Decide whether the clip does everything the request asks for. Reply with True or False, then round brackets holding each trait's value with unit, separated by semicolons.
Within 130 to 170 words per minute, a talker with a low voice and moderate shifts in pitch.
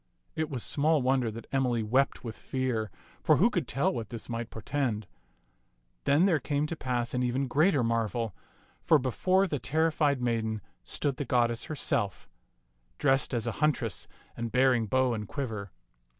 True (165 wpm; 130 Hz; 3.9 semitones)